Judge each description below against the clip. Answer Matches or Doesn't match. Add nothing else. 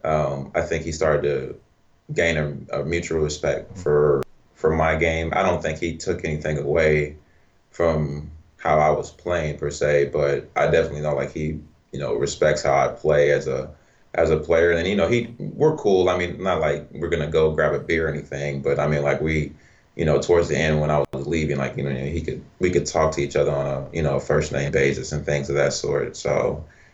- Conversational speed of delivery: Doesn't match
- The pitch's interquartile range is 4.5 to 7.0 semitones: Doesn't match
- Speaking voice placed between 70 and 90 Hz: Matches